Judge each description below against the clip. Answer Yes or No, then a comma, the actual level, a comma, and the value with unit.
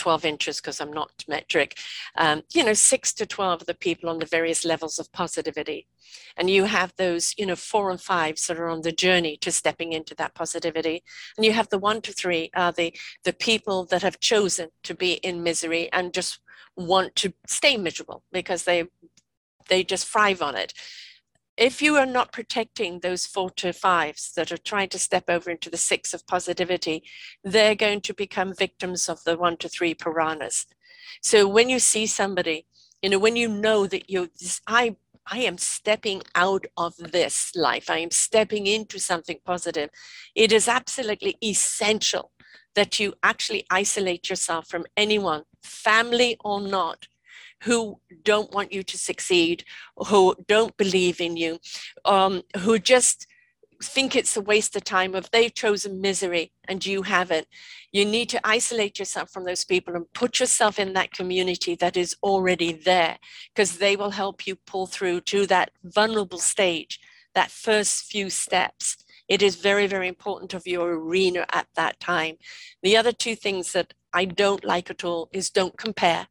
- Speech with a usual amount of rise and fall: Yes, average, 3.4 semitones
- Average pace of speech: Yes, average, 180 wpm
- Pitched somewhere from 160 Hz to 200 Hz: Yes, high, 190 Hz